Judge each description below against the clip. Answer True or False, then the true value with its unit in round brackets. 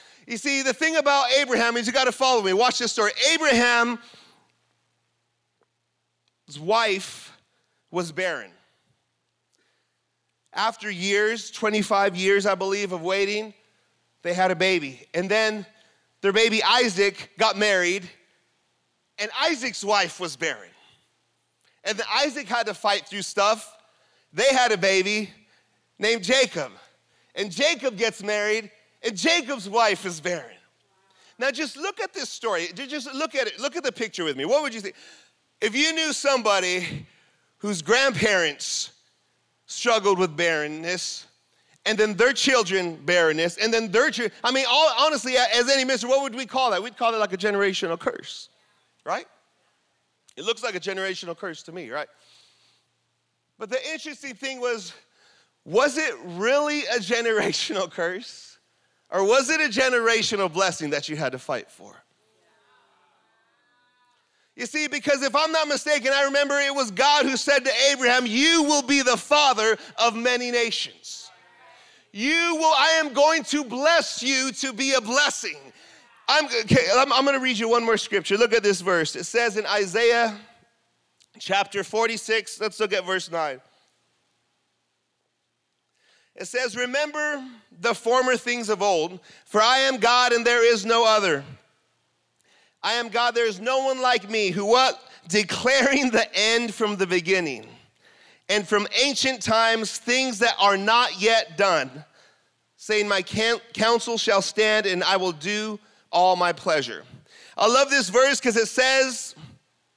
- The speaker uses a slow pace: False (150 wpm)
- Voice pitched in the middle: False (230 Hz)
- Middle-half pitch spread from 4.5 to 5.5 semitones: True (4.9 semitones)